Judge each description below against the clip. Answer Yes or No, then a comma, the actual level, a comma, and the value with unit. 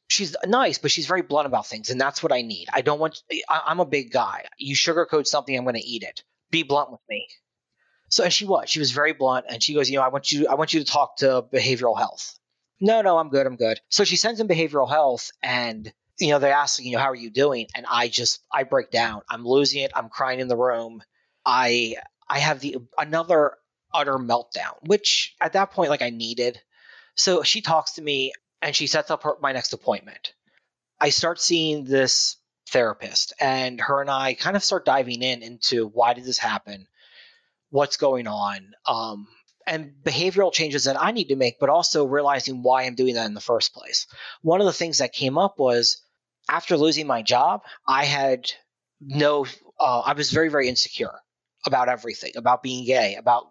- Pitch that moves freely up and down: No, average, 4.1 semitones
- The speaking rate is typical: No, fast, 215 wpm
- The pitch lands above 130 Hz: Yes, medium, 140 Hz